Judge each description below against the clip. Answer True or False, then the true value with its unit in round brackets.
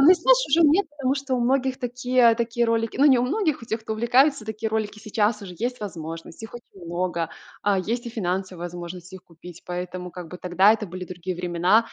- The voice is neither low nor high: False (220 Hz)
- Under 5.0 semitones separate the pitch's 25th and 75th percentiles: False (5.6 semitones)